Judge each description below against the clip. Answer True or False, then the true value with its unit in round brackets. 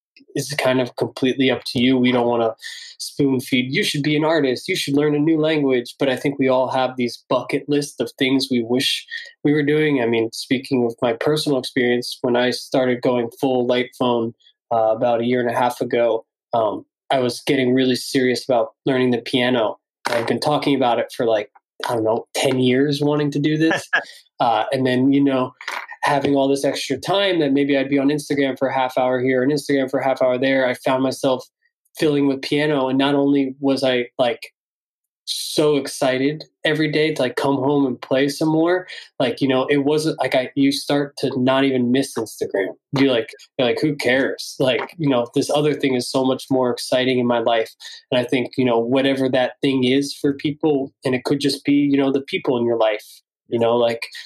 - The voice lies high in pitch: False (135 Hz)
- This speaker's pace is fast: True (220 wpm)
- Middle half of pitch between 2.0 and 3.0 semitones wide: True (2.4 semitones)